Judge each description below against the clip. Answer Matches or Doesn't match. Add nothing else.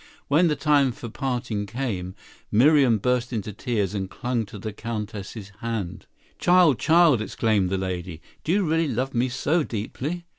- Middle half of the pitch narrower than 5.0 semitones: Doesn't match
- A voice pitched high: Doesn't match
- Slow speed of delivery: Doesn't match